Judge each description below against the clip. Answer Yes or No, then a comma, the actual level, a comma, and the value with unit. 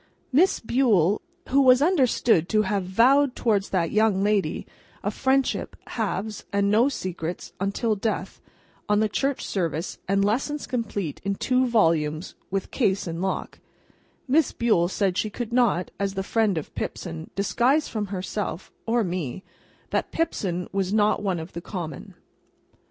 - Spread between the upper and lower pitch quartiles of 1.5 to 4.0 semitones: No, average, 4.5 semitones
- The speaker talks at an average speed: Yes, average, 145 wpm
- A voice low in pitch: No, high, 205 Hz